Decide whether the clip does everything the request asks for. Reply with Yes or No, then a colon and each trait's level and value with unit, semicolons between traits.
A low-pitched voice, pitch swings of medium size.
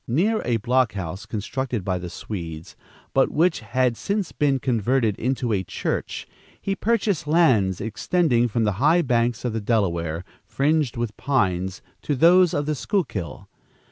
No: low, 120 Hz; wide, 6.6 semitones